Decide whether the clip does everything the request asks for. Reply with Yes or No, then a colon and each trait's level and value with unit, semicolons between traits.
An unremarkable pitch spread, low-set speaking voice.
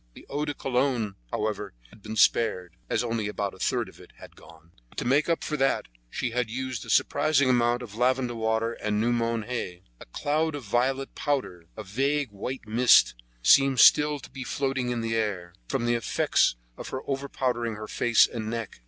Yes: average, 3.6 semitones; low, 120 Hz